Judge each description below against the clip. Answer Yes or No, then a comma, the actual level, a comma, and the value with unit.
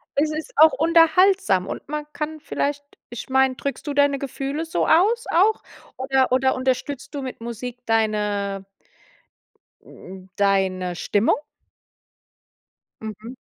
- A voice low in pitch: No, very high, 265 Hz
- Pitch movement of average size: No, wide, 5.9 semitones